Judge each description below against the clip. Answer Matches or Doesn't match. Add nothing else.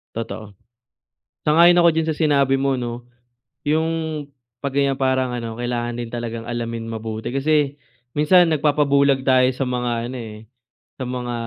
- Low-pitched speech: Matches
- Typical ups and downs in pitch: Matches